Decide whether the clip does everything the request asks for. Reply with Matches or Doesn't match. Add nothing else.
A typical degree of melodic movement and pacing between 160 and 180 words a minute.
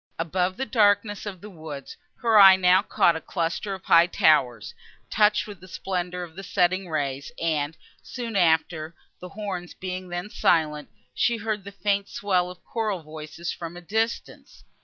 Matches